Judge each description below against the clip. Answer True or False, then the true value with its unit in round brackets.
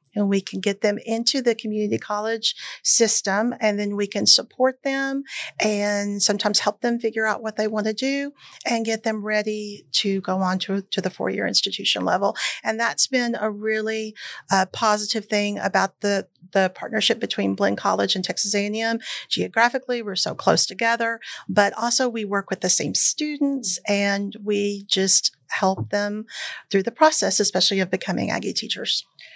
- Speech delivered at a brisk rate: False (170 wpm)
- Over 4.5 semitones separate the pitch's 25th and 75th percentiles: False (2.4 semitones)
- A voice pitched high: True (210 Hz)